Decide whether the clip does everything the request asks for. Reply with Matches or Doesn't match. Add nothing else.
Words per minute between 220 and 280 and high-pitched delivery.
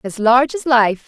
Matches